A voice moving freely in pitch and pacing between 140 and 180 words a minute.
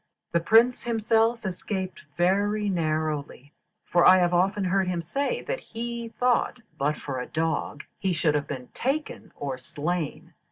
Yes: wide, 6.3 semitones; average, 155 wpm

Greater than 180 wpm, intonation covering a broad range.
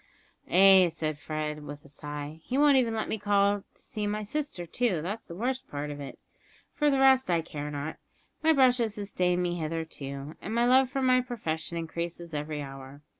Yes: average, 195 wpm; wide, 7.8 semitones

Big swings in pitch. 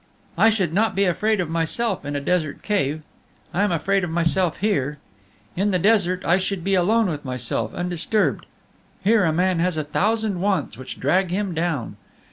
No: average, 3.9 semitones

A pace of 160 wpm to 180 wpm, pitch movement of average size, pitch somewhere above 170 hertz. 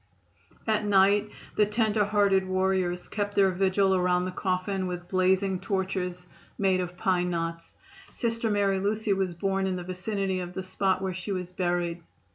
No: average, 165 wpm; narrow, 1.8 semitones; high, 190 Hz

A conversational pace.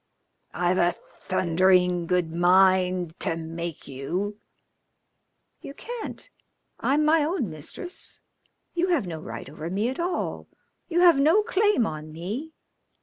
No: slow, 130 wpm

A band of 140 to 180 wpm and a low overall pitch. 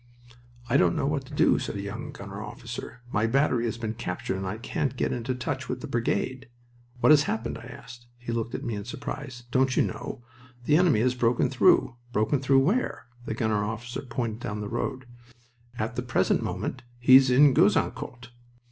No: average, 195 wpm; low, 120 Hz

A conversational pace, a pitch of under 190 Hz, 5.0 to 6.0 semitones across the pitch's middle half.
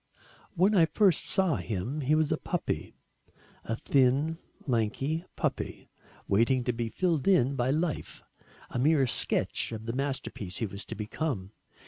Yes: average, 150 wpm; low, 135 Hz; wide, 5.6 semitones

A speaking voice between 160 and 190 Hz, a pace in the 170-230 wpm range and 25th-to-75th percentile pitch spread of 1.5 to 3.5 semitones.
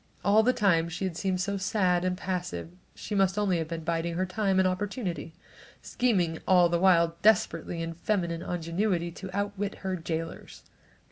Yes: medium, 185 Hz; average, 175 wpm; average, 2.8 semitones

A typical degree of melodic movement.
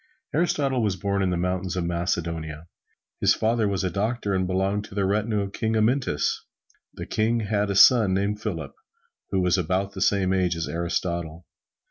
Yes: average, 3.1 semitones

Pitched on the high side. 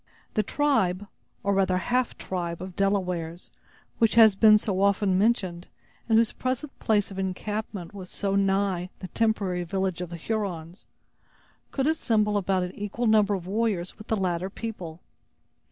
Yes: high, 195 Hz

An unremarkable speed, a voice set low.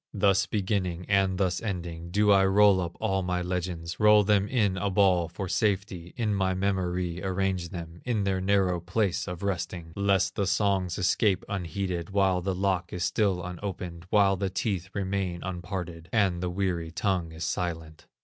Yes: average, 170 wpm; very low, 95 Hz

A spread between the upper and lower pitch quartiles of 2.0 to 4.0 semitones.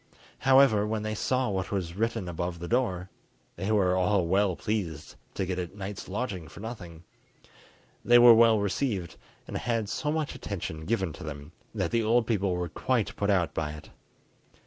No: average, 4.4 semitones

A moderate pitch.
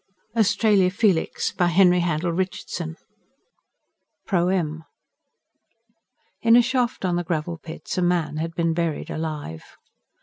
Yes: medium, 175 Hz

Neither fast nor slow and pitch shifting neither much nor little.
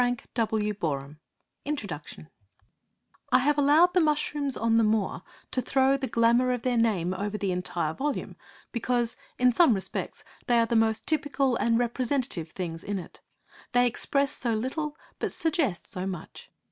Yes: average, 165 wpm; average, 5.0 semitones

